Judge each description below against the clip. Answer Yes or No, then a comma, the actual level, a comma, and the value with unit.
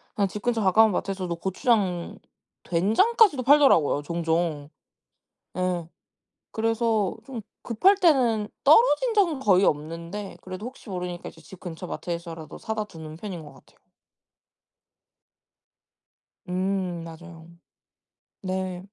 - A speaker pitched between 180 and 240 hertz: Yes, high, 190 Hz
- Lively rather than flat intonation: No, average, 4.9 semitones